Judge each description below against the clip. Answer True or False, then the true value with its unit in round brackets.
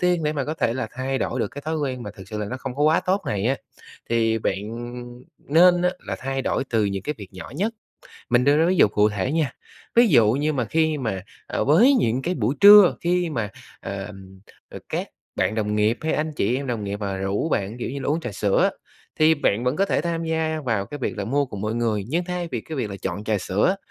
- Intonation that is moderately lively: False (7.0 semitones)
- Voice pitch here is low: True (130 Hz)